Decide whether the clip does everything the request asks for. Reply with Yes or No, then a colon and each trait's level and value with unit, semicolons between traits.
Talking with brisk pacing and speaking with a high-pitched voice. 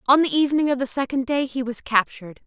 Yes: fast, 245 wpm; very high, 260 Hz